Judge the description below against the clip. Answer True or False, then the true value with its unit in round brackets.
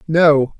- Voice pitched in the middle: True (155 Hz)